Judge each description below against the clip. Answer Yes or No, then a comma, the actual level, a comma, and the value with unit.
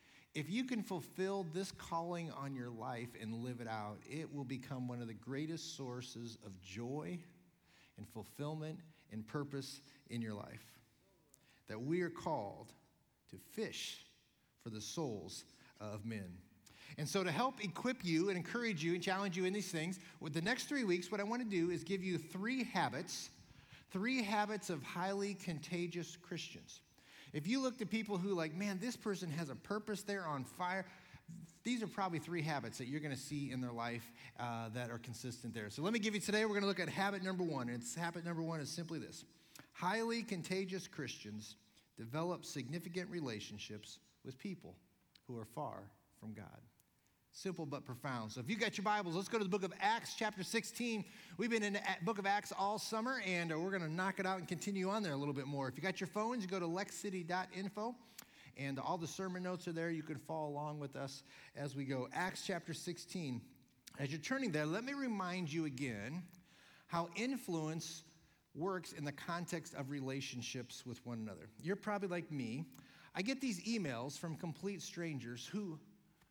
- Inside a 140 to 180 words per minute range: No, average, 195 wpm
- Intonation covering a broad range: Yes, wide, 6.2 semitones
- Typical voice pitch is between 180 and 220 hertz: No, medium, 170 Hz